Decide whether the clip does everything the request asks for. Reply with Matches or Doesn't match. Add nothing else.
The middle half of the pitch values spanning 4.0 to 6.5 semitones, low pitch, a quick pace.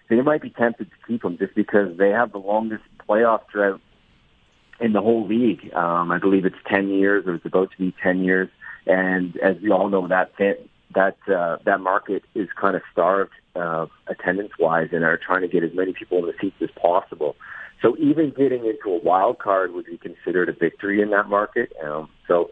Matches